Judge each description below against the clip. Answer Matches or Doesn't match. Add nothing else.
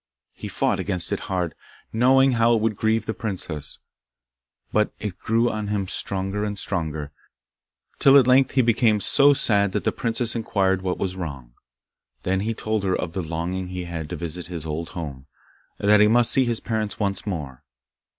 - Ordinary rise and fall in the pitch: Matches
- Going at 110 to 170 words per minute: Doesn't match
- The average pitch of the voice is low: Matches